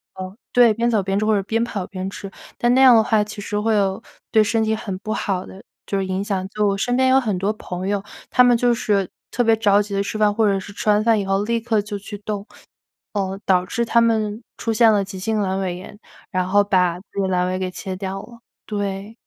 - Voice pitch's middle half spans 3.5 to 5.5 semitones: No, narrow, 2.4 semitones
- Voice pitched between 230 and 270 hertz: No, high, 205 Hz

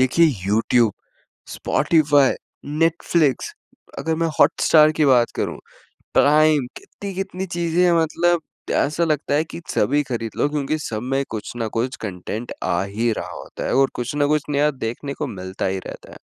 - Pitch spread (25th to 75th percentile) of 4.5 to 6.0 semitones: Yes, average, 5.2 semitones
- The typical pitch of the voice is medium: Yes, medium, 145 Hz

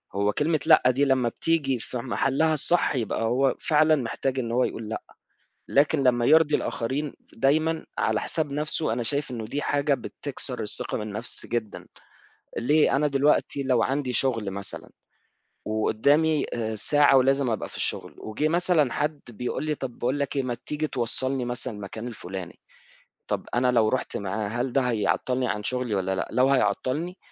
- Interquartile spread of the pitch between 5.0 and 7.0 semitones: No, average, 4.1 semitones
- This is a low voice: Yes, low, 130 Hz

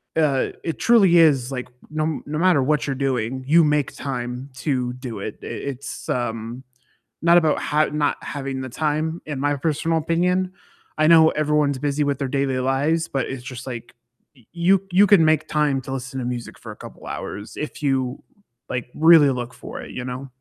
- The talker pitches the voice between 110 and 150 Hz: Yes, medium, 140 Hz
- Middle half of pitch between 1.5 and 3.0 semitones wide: No, average, 3.5 semitones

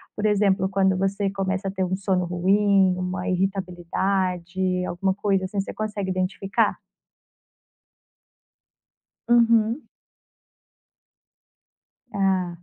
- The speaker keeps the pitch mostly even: Yes, narrow, 1.4 semitones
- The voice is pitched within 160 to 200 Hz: Yes, high, 190 Hz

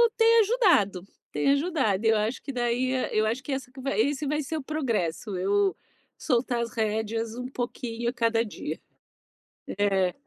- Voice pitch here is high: Yes, high, 235 Hz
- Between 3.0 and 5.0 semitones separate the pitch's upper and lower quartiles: Yes, average, 4.1 semitones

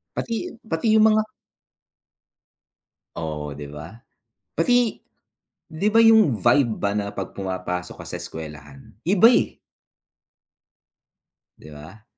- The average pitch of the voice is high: No, low, 105 Hz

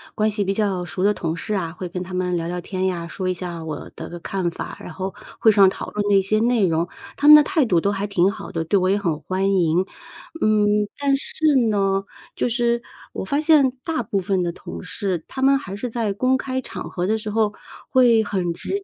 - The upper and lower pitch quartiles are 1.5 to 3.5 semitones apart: No, average, 3.9 semitones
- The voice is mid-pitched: No, high, 195 Hz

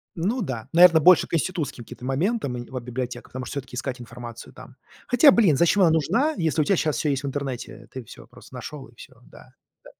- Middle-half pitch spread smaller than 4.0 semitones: No, wide, 5.5 semitones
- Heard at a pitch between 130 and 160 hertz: Yes, medium, 140 Hz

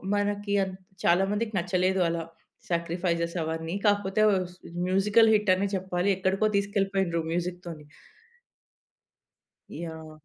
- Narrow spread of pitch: No, average, 3.0 semitones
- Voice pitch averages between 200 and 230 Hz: No, medium, 185 Hz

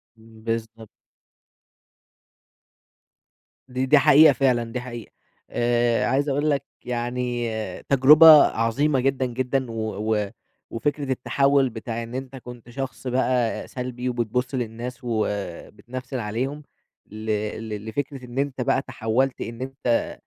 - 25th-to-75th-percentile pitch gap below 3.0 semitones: Yes, narrow, 2.6 semitones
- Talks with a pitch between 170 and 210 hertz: No, low, 125 Hz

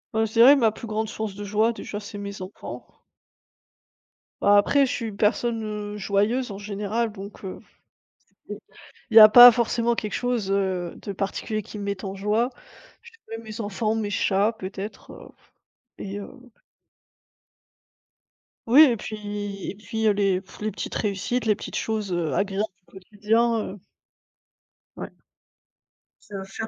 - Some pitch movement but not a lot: No, narrow, 2.0 semitones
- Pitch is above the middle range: Yes, high, 210 Hz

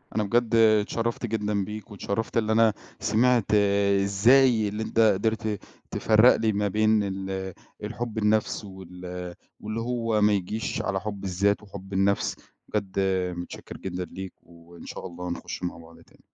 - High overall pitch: No, low, 105 Hz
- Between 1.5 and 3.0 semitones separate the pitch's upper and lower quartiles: Yes, narrow, 2.6 semitones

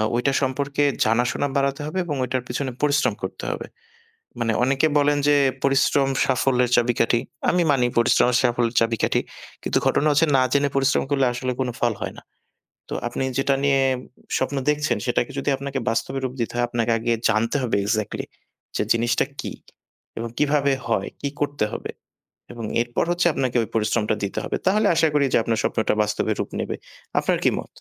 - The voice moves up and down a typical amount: Yes, average, 3.2 semitones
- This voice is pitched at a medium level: No, low, 130 Hz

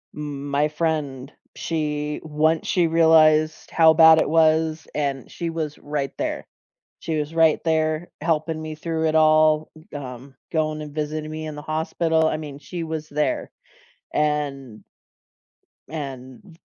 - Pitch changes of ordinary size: No, narrow, 1.3 semitones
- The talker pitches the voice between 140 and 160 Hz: Yes, medium, 155 Hz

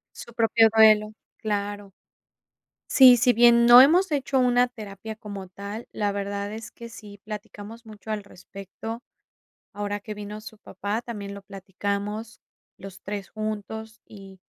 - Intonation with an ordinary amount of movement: No, narrow, 2.1 semitones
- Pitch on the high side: Yes, high, 215 Hz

